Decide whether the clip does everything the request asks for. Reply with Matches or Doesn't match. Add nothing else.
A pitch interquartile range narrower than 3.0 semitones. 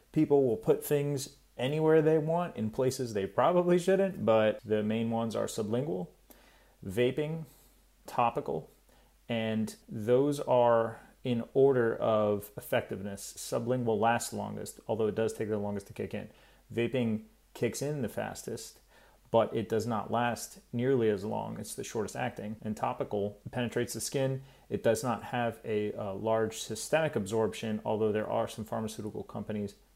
Doesn't match